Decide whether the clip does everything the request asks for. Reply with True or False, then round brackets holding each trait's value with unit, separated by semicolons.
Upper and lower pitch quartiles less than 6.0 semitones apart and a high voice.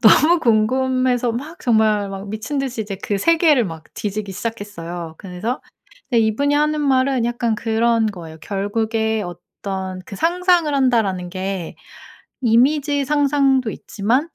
True (5.2 semitones; 230 Hz)